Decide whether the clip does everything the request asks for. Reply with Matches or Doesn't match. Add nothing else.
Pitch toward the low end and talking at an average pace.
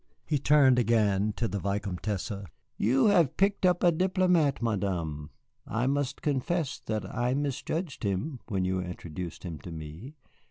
Matches